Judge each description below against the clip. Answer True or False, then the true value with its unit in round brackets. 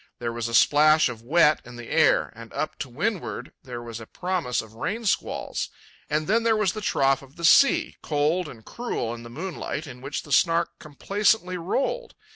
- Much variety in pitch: True (7.0 semitones)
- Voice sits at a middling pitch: True (155 Hz)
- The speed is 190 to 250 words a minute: True (200 wpm)